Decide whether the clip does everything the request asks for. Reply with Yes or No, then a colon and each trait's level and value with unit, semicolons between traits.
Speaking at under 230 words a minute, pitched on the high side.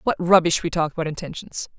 No: average, 200 wpm; medium, 170 Hz